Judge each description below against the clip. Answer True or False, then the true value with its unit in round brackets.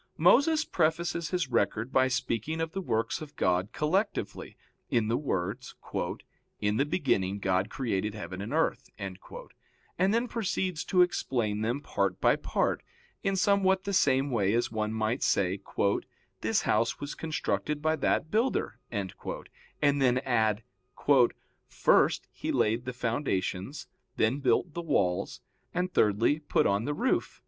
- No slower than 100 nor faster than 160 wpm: True (145 wpm)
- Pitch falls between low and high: False (130 Hz)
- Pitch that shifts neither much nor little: False (7.4 semitones)